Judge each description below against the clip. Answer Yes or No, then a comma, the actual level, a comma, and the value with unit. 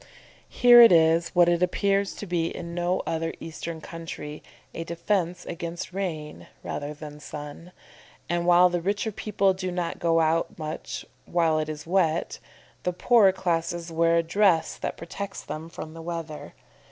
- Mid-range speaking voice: Yes, medium, 170 Hz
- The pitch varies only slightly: Yes, narrow, 1.8 semitones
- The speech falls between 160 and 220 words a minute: Yes, average, 165 wpm